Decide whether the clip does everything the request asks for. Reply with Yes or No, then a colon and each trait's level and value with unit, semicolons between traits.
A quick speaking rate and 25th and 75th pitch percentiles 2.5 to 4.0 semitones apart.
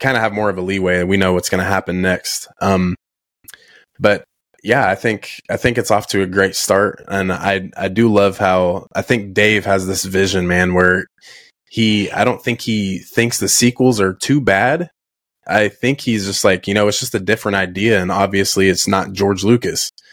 Yes: fast, 210 wpm; average, 2.8 semitones